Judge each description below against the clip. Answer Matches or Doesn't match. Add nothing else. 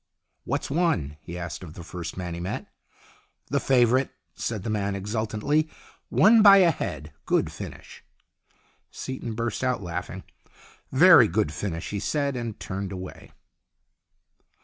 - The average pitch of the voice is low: Matches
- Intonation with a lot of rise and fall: Matches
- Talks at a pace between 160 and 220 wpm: Doesn't match